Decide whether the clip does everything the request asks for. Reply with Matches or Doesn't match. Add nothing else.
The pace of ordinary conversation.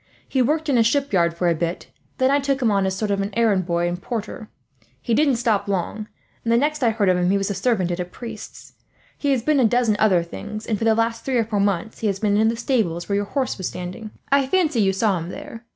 Doesn't match